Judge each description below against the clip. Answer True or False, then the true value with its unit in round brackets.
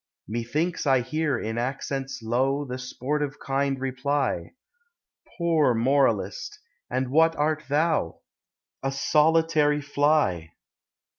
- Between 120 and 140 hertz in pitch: True (135 Hz)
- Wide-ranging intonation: False (3.0 semitones)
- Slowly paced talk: True (100 wpm)